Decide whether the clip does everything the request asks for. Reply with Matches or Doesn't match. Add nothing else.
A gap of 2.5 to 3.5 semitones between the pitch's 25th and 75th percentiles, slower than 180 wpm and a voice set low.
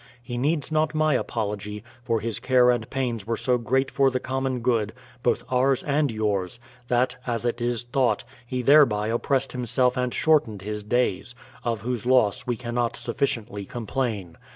Matches